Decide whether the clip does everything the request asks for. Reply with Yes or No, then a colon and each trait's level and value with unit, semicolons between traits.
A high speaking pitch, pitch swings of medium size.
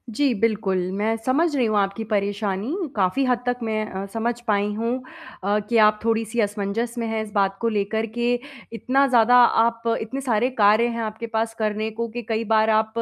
No: high, 220 Hz; narrow, 2.0 semitones